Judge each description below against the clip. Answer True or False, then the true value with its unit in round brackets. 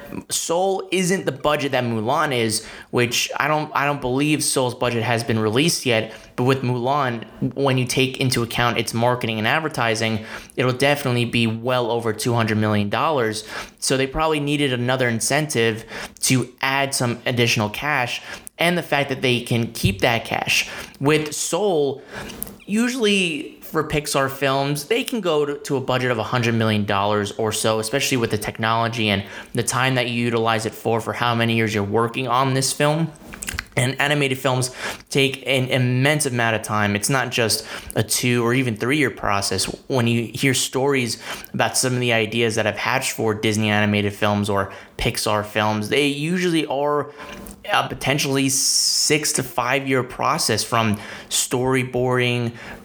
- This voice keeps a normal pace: True (170 wpm)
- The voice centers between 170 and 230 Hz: False (125 Hz)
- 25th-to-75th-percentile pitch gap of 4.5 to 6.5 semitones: False (3.5 semitones)